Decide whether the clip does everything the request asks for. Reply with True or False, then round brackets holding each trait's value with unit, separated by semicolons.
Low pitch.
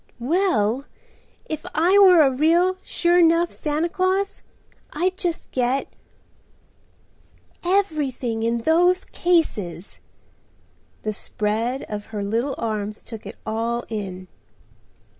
False (275 Hz)